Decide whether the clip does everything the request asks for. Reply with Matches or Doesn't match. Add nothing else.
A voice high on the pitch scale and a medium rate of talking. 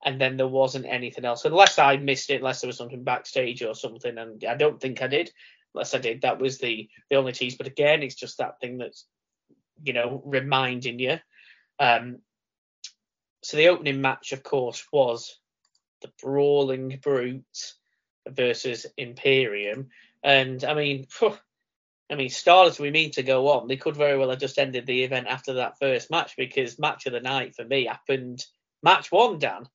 Doesn't match